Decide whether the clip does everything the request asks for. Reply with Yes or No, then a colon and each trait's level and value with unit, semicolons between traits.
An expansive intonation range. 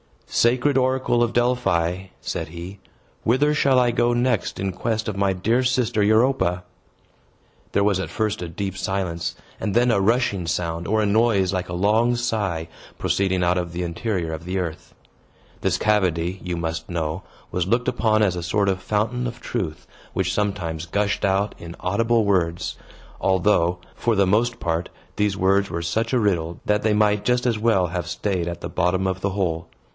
No: average, 4.3 semitones